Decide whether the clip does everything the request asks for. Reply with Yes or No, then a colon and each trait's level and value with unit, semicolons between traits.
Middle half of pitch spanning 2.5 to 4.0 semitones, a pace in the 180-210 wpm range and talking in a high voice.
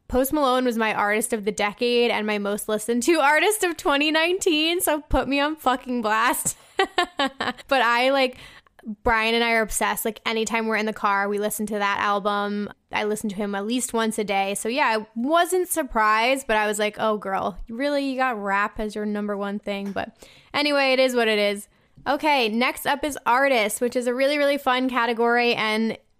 No: average, 4.4 semitones; fast, 205 wpm; high, 235 Hz